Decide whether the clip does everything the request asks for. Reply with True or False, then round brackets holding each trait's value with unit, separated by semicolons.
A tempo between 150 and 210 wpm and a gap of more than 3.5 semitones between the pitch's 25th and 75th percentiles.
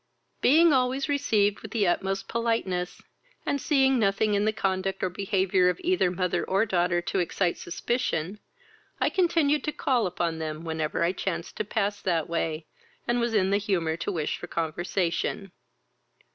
True (165 wpm; 4.8 semitones)